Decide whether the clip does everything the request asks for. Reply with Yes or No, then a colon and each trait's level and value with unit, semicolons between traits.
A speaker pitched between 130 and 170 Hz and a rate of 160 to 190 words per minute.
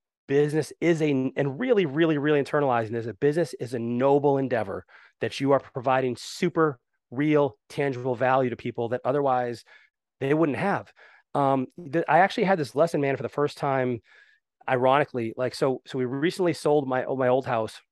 Yes: low, 135 Hz; average, 175 wpm